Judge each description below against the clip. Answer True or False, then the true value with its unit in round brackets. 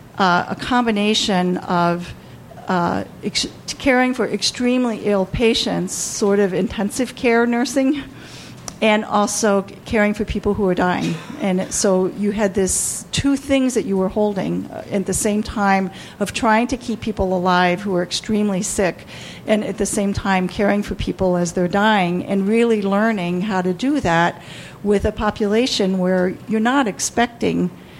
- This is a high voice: True (205 Hz)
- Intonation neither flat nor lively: True (3.0 semitones)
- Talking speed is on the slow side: False (165 wpm)